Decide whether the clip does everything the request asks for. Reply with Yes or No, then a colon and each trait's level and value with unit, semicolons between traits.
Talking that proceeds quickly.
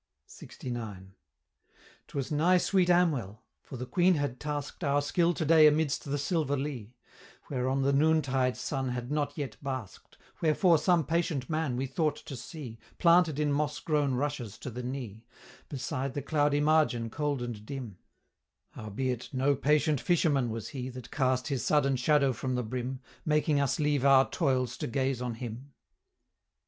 No: average, 160 wpm